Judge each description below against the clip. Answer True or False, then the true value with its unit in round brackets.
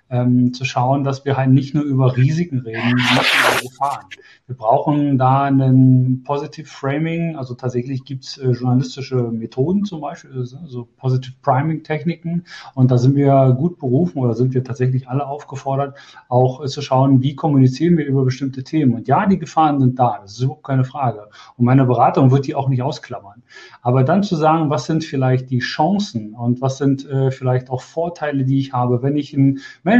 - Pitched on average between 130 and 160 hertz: True (135 Hz)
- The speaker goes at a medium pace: False (195 wpm)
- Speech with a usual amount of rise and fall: False (2.3 semitones)